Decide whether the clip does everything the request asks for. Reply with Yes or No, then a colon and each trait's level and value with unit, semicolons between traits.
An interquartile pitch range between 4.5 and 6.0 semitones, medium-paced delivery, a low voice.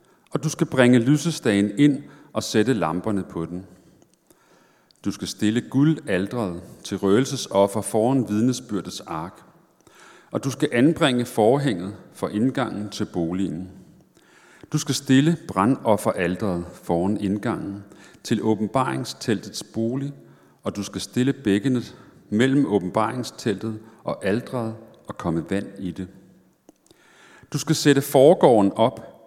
No: average, 5.2 semitones; slow, 115 wpm; low, 110 Hz